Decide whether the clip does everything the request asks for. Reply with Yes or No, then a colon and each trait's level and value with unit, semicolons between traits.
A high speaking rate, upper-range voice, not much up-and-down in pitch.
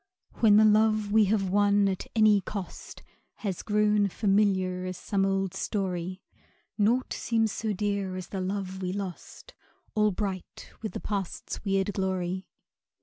No: average, 145 wpm; high, 200 Hz; narrow, 2.0 semitones